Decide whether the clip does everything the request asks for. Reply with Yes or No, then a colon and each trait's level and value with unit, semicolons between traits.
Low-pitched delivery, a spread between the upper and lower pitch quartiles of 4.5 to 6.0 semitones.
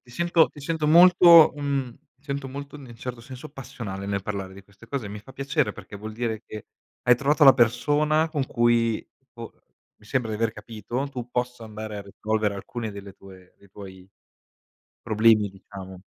Yes: low, 115 Hz; average, 4.9 semitones